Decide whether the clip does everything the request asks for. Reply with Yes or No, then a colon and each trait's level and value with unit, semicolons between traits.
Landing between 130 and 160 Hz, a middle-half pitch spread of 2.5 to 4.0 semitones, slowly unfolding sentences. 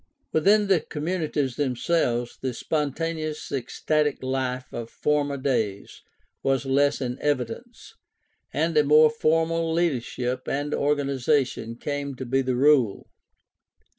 Yes: medium, 140 Hz; average, 3.2 semitones; slow, 120 wpm